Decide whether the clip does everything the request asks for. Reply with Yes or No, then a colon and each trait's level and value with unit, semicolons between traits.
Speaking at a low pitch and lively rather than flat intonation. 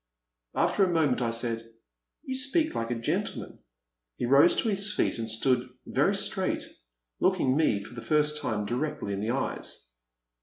Yes: low, 125 Hz; wide, 6.2 semitones